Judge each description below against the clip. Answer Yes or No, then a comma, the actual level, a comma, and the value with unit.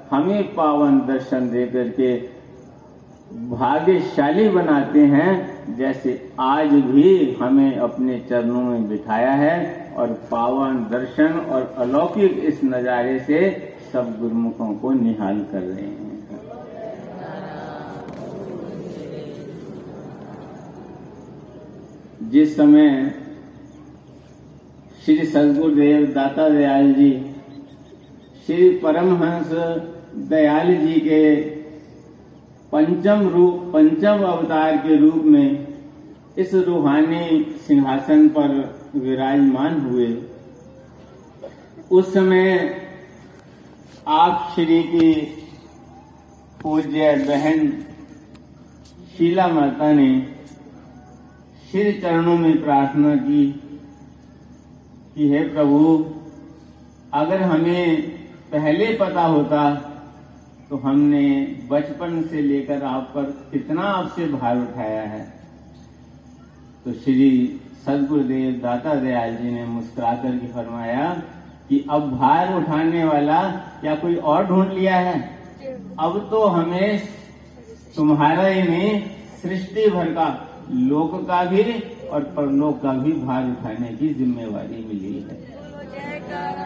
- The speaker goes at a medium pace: No, slow, 95 wpm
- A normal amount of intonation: No, wide, 5.9 semitones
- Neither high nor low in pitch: Yes, medium, 155 Hz